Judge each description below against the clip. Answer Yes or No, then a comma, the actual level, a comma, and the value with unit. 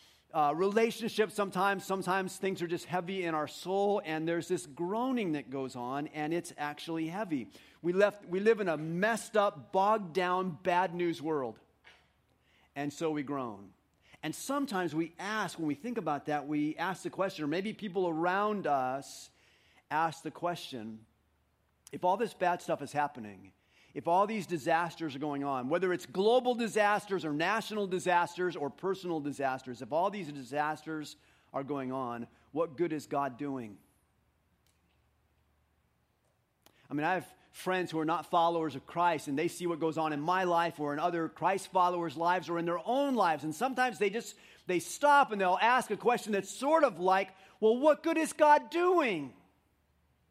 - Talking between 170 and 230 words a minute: Yes, average, 175 wpm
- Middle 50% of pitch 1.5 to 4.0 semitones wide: No, average, 5.1 semitones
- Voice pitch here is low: No, medium, 170 Hz